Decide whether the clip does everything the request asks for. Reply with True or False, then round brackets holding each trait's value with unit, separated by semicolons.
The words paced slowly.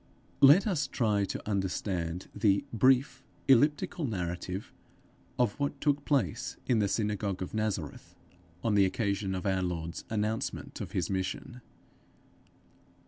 True (130 wpm)